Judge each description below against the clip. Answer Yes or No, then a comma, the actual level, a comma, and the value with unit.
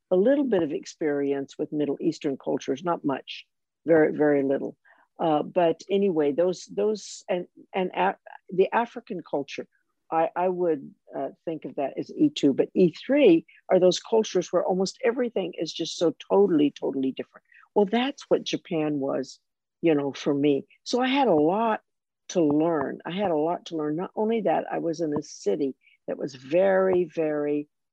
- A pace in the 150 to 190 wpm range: Yes, average, 175 wpm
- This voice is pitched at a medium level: Yes, medium, 175 Hz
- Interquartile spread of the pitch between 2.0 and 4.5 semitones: No, average, 4.9 semitones